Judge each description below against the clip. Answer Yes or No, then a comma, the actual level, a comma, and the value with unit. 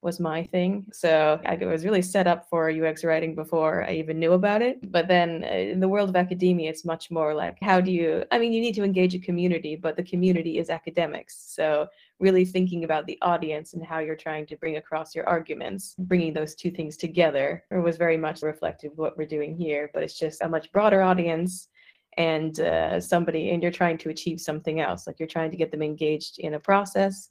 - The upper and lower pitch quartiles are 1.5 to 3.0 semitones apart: Yes, narrow, 2.5 semitones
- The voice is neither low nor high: Yes, medium, 165 Hz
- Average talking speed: No, fast, 225 wpm